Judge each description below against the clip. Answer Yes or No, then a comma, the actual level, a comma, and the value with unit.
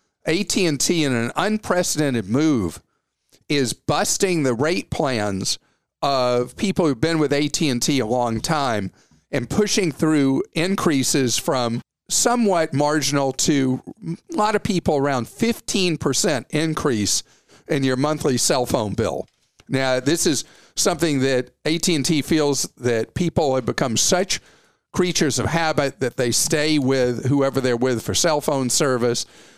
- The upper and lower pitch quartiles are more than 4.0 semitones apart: Yes, average, 4.6 semitones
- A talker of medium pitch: Yes, medium, 145 Hz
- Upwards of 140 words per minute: No, slow, 135 wpm